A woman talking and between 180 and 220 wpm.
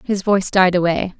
Yes: female; average, 200 wpm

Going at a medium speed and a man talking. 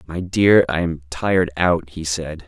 Yes: average, 195 wpm; male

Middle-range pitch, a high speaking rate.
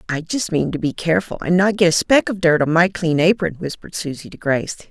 Yes: medium, 170 Hz; fast, 255 wpm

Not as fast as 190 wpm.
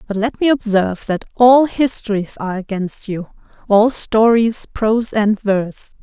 Yes: average, 140 wpm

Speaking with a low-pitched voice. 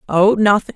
No: high, 200 Hz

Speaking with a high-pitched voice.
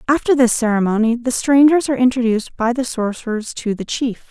Yes: high, 240 Hz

